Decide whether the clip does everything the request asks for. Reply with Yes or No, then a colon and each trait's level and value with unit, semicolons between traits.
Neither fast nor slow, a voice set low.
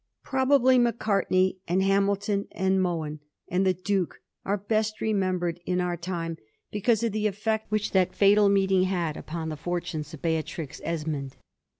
No: average, 160 wpm; high, 190 Hz